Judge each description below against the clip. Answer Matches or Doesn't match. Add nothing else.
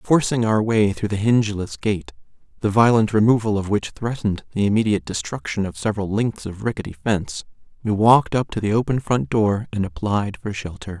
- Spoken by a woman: Doesn't match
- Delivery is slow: Doesn't match